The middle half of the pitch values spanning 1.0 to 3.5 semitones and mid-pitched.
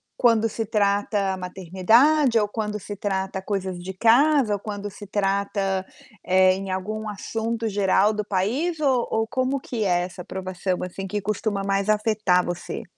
No: narrow, 2.6 semitones; high, 205 Hz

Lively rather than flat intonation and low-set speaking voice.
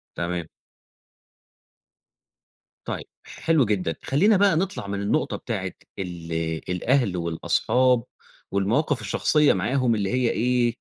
Yes: wide, 6.3 semitones; low, 115 Hz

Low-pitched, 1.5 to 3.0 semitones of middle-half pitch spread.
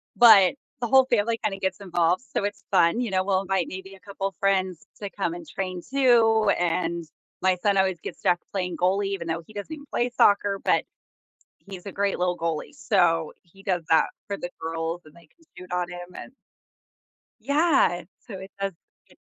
No: high, 190 Hz; narrow, 2.6 semitones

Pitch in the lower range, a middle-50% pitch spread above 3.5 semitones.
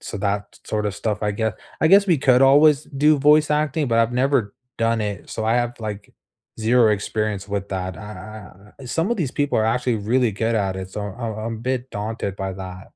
Yes: low, 110 Hz; average, 4.2 semitones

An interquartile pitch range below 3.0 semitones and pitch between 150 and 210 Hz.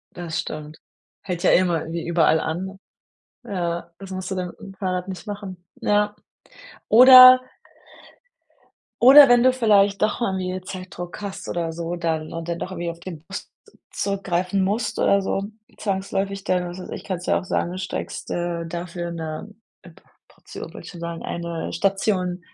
Yes: narrow, 2.6 semitones; medium, 185 Hz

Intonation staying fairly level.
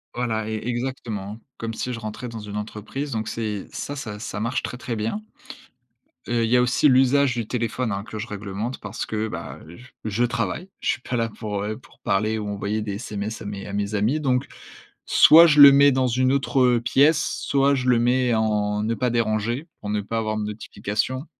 No: average, 3.2 semitones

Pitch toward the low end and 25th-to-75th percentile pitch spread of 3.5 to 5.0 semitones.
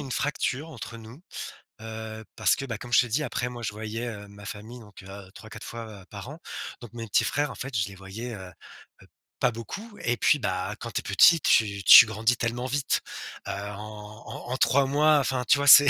Yes: low, 115 Hz; average, 3.8 semitones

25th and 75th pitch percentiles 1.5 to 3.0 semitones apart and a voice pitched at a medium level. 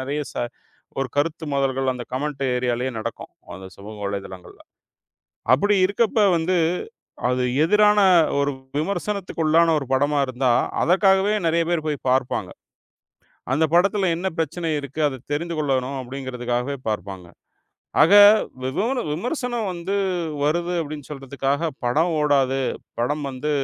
No: average, 4.8 semitones; medium, 145 Hz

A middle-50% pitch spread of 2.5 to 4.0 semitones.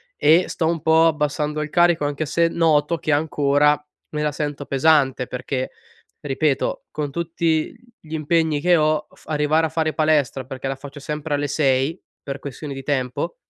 No: narrow, 2.1 semitones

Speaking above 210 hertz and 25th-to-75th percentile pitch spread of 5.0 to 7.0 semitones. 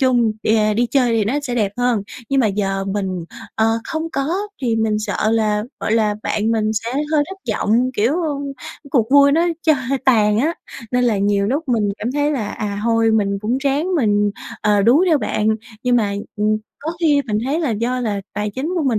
No: high, 225 Hz; average, 4.2 semitones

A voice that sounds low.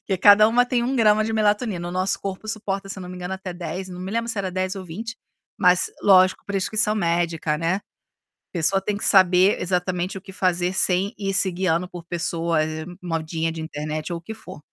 No: medium, 185 Hz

